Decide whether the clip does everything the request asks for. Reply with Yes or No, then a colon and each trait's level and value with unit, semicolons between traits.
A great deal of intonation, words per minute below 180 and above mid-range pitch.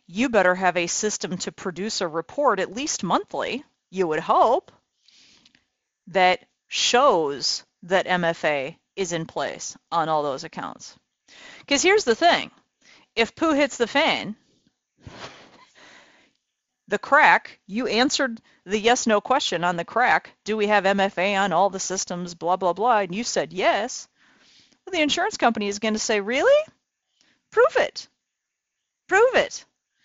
Yes: wide, 6.6 semitones; average, 150 wpm; high, 210 Hz